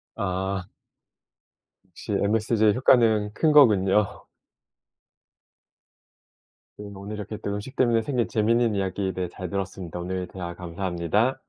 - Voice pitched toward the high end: No, low, 100 Hz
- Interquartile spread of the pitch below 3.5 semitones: Yes, average, 3.1 semitones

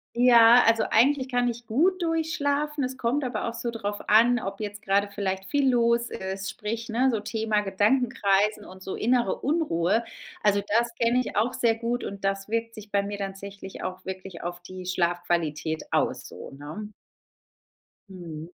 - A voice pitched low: No, high, 215 Hz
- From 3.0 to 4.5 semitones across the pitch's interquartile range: Yes, average, 4.0 semitones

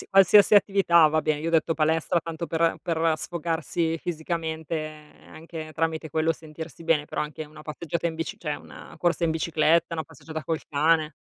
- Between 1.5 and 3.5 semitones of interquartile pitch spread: No, narrow, 1.1 semitones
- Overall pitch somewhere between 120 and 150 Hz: No, medium, 160 Hz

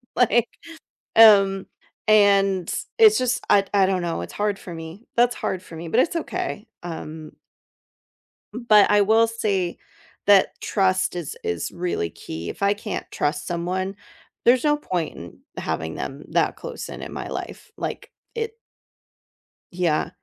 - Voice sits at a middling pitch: No, high, 195 Hz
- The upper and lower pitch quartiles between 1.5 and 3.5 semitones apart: No, average, 4.8 semitones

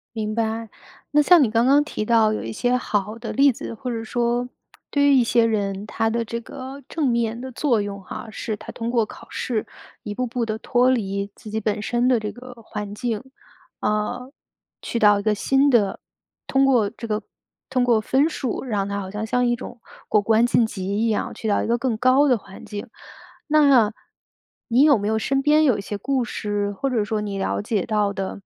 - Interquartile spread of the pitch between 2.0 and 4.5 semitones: Yes, average, 3.1 semitones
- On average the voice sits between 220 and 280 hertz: Yes, high, 230 Hz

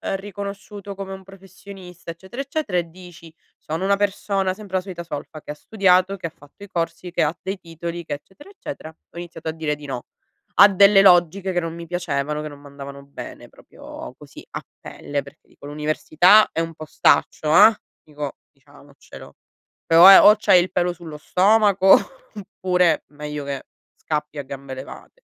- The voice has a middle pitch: Yes, medium, 175 Hz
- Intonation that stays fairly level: No, average, 4.2 semitones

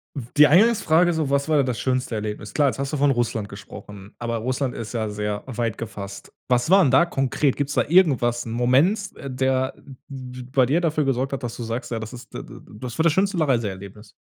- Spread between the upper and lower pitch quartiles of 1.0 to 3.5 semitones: No, average, 4.1 semitones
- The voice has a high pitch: No, low, 130 Hz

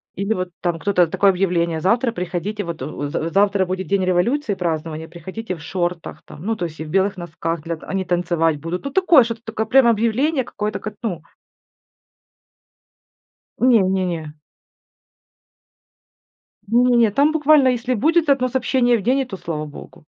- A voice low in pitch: No, high, 195 Hz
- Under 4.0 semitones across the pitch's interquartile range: No, wide, 5.6 semitones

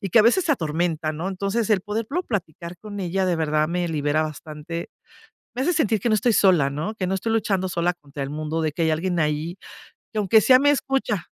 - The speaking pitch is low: No, medium, 180 Hz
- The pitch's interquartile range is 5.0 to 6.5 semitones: Yes, wide, 5.4 semitones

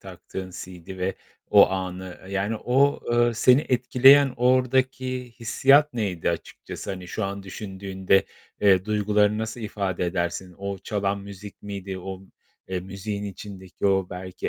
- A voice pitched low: Yes, low, 100 Hz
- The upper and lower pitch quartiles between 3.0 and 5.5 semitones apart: Yes, average, 3.6 semitones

